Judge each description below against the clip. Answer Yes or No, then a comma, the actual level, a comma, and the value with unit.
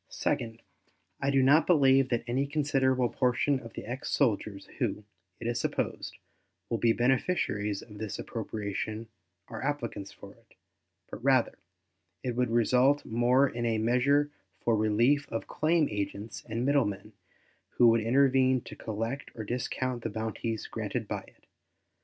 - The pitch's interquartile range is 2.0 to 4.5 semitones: Yes, average, 3.4 semitones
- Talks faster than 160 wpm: No, average, 150 wpm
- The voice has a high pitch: No, low, 120 Hz